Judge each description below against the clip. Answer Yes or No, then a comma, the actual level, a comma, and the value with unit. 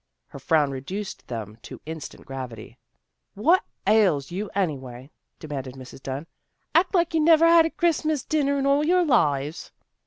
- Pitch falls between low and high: Yes, medium, 180 Hz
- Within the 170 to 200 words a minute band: Yes, average, 175 wpm